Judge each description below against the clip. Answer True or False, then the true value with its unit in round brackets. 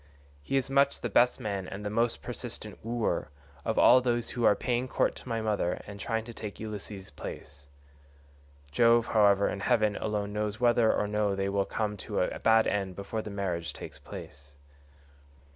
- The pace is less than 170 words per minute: False (185 wpm)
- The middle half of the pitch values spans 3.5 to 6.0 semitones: False (2.8 semitones)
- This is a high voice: False (105 Hz)